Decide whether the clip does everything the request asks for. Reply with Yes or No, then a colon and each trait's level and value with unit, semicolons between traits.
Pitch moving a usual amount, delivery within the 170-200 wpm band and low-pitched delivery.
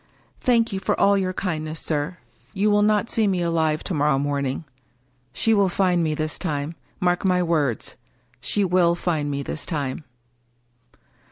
No: average, 4.2 semitones; average, 175 wpm; medium, 170 Hz